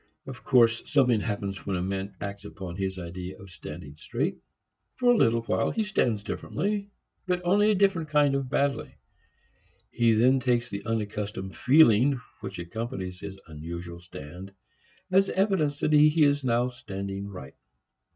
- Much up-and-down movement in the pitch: Yes, wide, 6.8 semitones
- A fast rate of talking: No, average, 155 wpm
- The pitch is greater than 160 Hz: No, low, 115 Hz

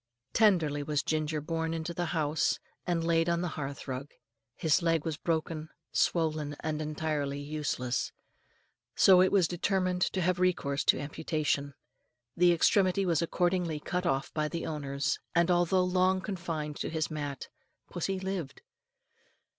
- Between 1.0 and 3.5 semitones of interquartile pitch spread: Yes, average, 2.9 semitones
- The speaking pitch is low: No, medium, 160 Hz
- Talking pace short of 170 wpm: Yes, average, 145 wpm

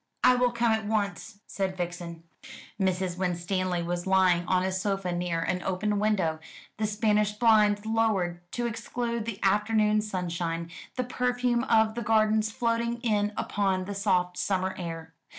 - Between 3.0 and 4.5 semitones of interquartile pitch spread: Yes, average, 3.5 semitones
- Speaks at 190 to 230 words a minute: No, average, 150 wpm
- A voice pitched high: Yes, high, 200 Hz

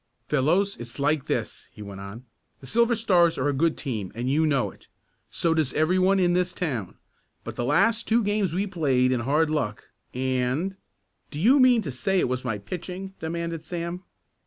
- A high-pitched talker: No, medium, 160 Hz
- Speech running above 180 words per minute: Yes, average, 200 wpm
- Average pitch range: No, wide, 6.3 semitones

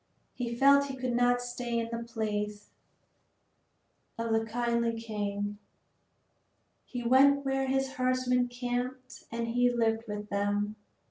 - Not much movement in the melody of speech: Yes, narrow, 2.2 semitones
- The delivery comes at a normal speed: No, slow, 130 wpm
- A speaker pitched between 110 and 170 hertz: No, high, 240 Hz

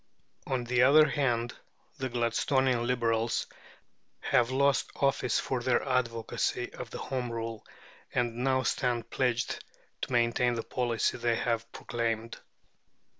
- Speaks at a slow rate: Yes, slow, 125 wpm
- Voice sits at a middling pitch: No, low, 120 Hz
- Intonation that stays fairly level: Yes, narrow, 1.7 semitones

